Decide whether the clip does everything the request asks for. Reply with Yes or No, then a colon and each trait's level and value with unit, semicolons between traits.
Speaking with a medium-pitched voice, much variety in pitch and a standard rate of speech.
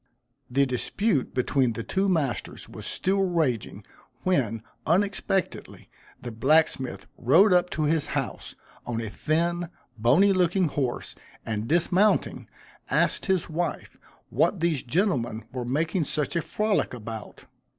No: medium, 155 Hz; wide, 6.7 semitones; slow, 130 wpm